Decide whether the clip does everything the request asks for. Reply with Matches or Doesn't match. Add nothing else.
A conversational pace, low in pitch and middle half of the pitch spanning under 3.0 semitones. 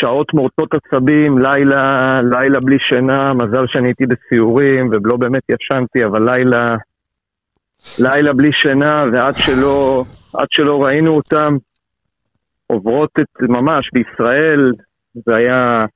Matches